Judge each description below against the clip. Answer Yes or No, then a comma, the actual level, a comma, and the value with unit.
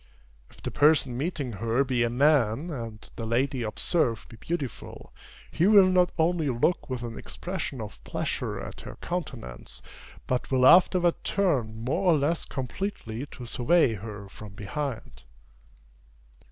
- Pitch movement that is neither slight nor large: No, wide, 6.5 semitones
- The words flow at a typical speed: Yes, average, 145 wpm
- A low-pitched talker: Yes, low, 130 Hz